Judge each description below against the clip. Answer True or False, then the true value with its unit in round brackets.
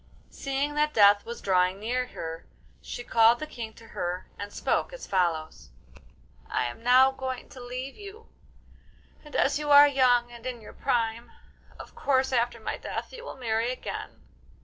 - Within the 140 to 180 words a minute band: True (170 wpm)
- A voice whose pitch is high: True (245 Hz)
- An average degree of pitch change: True (3.5 semitones)